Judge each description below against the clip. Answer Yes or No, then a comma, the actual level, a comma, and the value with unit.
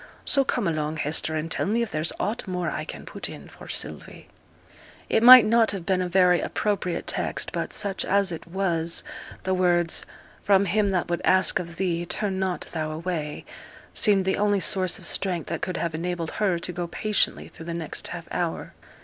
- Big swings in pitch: No, average, 2.8 semitones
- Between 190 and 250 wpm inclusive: Yes, average, 200 wpm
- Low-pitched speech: No, medium, 180 Hz